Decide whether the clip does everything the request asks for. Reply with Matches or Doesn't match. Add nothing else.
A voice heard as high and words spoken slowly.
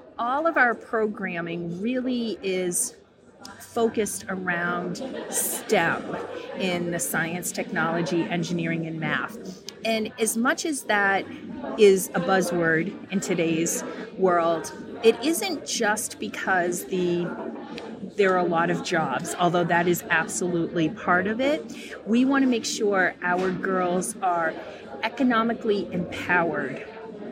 Matches